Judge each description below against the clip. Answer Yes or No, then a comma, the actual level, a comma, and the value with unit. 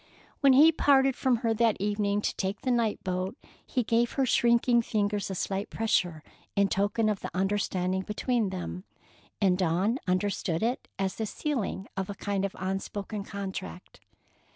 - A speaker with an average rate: Yes, average, 165 wpm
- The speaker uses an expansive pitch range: No, average, 3.5 semitones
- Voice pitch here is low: No, high, 205 Hz